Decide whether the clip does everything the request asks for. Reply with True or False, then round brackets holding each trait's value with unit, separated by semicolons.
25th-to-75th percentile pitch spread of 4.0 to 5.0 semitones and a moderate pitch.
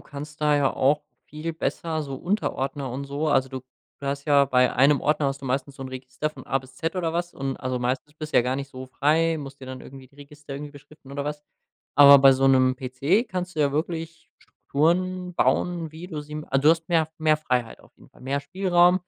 False (2.9 semitones; 145 Hz)